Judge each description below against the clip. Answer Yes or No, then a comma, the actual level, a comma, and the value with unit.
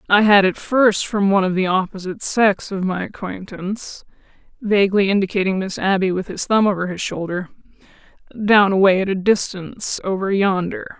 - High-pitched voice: Yes, high, 195 Hz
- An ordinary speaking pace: Yes, average, 165 wpm